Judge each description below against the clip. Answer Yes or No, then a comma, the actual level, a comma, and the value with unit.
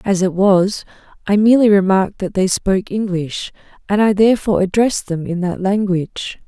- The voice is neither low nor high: No, high, 195 Hz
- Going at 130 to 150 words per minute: No, average, 165 wpm